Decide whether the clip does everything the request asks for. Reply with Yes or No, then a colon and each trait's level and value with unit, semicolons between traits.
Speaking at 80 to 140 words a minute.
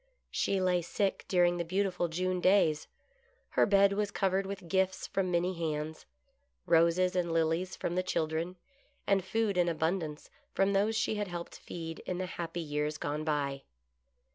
No: average, 165 wpm